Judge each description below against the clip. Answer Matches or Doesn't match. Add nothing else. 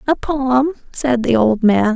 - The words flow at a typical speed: Matches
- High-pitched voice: Matches